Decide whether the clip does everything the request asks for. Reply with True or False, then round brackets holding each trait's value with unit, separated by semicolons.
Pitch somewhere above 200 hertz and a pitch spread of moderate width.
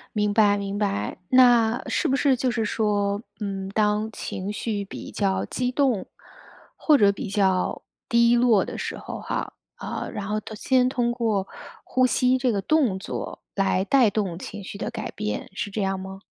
True (210 Hz; 3.5 semitones)